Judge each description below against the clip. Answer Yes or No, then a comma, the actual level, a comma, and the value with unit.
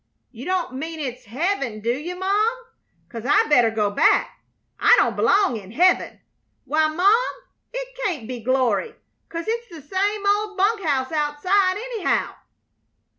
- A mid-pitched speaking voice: No, very high, 335 Hz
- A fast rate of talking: No, average, 150 wpm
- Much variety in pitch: Yes, wide, 7.9 semitones